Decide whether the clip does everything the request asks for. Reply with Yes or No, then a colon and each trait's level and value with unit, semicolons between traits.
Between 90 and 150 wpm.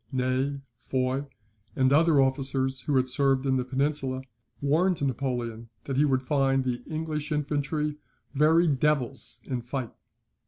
Yes: average, 140 wpm